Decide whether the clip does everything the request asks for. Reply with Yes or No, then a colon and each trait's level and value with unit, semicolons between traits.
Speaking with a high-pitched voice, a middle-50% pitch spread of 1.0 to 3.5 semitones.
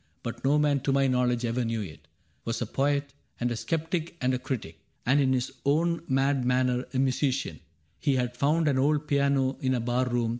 No: low, 130 Hz; narrow, 2.4 semitones